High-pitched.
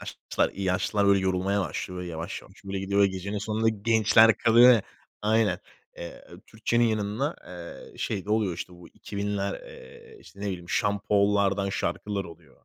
No: low, 100 Hz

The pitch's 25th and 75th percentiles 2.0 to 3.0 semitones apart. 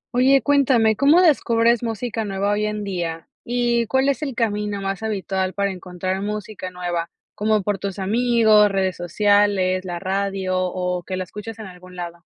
No: average, 3.5 semitones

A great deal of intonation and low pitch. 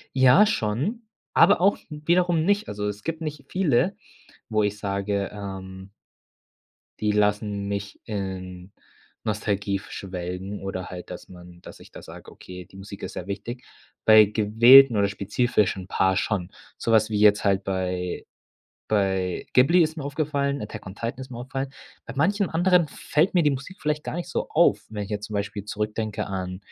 Yes: wide, 6.2 semitones; low, 105 Hz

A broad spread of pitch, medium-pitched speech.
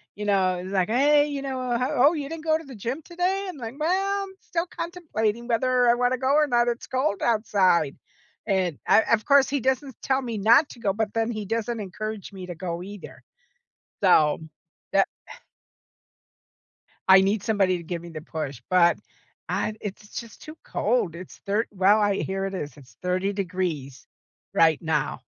No: wide, 5.9 semitones; high, 215 Hz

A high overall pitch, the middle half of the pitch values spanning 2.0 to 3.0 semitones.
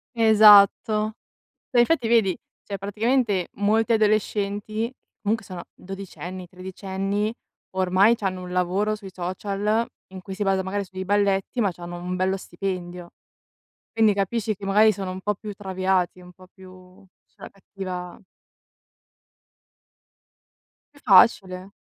Yes: high, 195 Hz; narrow, 2.4 semitones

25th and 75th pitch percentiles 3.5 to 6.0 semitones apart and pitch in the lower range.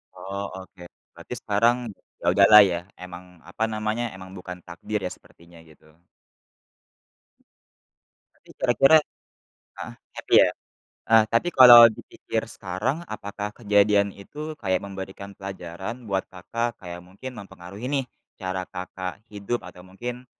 Yes: average, 3.9 semitones; low, 100 Hz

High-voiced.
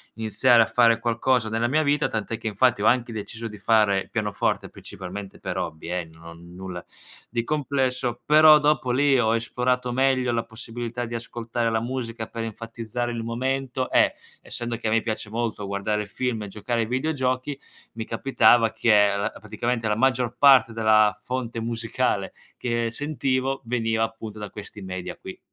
No: low, 115 Hz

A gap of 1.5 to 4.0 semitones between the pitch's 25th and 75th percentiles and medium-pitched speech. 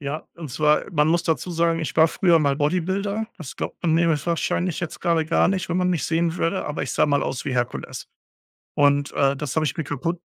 Yes: average, 2.8 semitones; medium, 165 Hz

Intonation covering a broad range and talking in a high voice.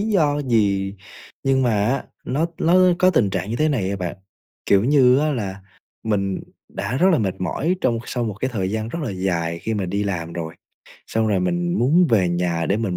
No: wide, 6.0 semitones; low, 110 Hz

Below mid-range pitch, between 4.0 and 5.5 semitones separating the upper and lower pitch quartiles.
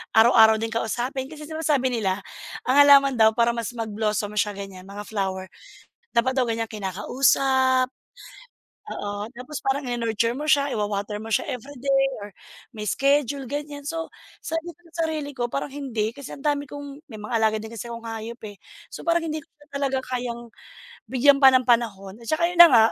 No: very high, 250 Hz; average, 4.3 semitones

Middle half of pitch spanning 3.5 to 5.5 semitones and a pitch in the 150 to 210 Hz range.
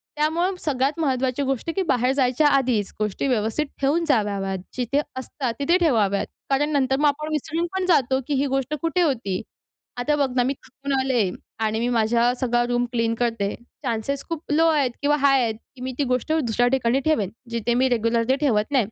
No: average, 3.9 semitones; very high, 260 Hz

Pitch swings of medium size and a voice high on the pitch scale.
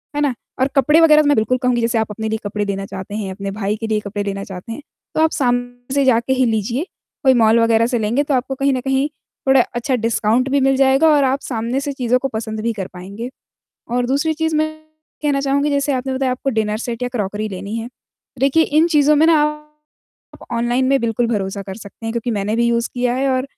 Yes: average, 3.8 semitones; high, 245 Hz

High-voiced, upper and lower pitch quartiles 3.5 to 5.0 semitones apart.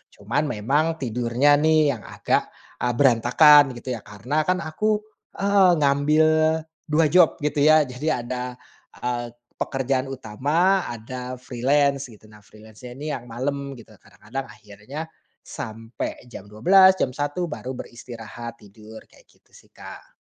No: low, 130 Hz; average, 4.2 semitones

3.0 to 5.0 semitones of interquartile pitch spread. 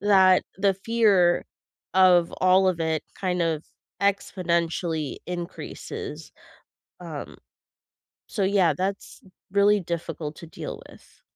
No: narrow, 2.6 semitones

